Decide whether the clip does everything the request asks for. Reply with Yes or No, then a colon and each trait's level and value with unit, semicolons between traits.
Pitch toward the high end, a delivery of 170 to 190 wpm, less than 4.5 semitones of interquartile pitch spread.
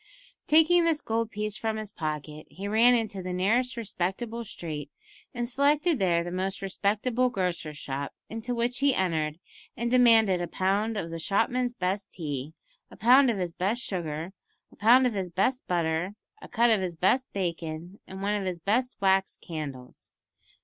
No: high, 200 Hz; average, 175 wpm; wide, 5.5 semitones